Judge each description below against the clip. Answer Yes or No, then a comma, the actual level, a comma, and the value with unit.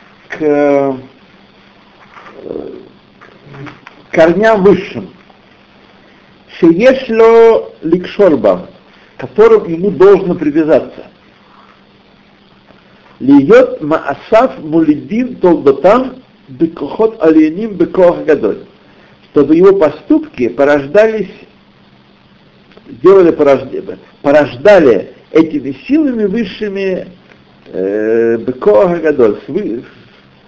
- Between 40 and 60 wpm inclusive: Yes, slow, 55 wpm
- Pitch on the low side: No, high, 200 Hz